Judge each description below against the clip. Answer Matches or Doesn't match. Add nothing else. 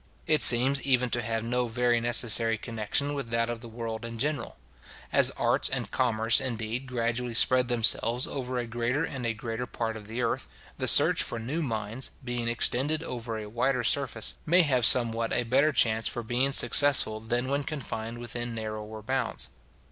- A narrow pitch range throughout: Matches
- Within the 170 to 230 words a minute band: Matches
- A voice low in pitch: Matches